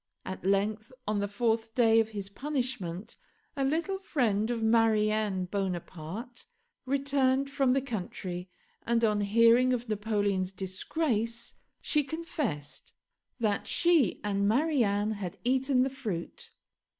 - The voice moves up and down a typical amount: Yes, average, 4.6 semitones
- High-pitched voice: Yes, high, 225 Hz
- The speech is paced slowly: Yes, slow, 125 wpm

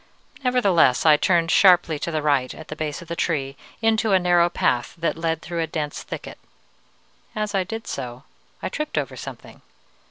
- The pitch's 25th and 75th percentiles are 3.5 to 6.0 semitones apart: Yes, average, 3.9 semitones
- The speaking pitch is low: No, medium, 165 Hz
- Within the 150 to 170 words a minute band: No, average, 185 wpm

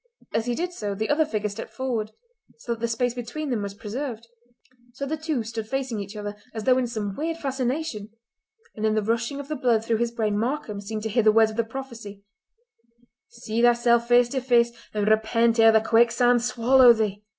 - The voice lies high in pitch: Yes, high, 235 Hz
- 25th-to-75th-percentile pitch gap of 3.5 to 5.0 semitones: No, average, 2.8 semitones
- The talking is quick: Yes, fast, 210 wpm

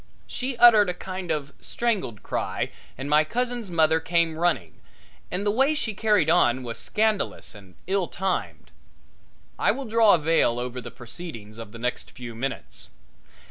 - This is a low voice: No, medium, 170 Hz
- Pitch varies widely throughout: Yes, wide, 8.9 semitones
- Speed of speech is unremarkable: Yes, average, 170 wpm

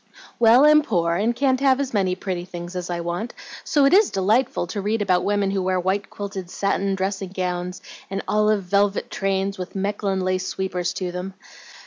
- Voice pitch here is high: Yes, high, 195 Hz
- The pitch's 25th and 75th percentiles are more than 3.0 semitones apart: No, narrow, 2.5 semitones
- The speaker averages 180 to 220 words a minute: Yes, average, 190 wpm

